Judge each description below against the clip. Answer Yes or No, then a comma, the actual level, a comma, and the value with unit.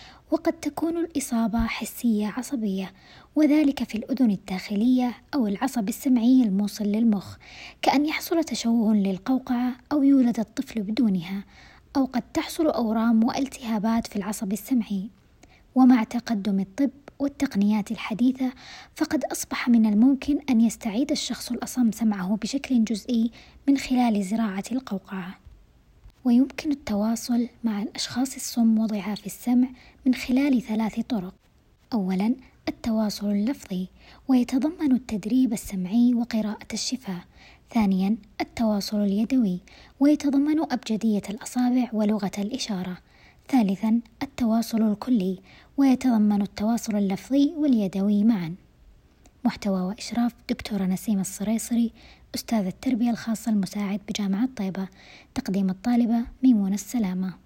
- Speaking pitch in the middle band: No, high, 230 Hz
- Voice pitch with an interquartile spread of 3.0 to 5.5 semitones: Yes, average, 3.7 semitones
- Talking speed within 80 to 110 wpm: Yes, average, 105 wpm